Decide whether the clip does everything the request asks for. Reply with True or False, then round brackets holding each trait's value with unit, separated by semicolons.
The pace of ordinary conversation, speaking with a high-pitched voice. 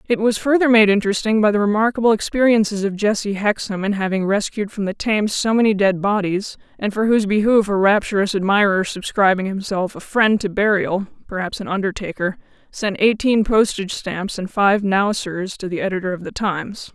True (185 wpm; 205 Hz)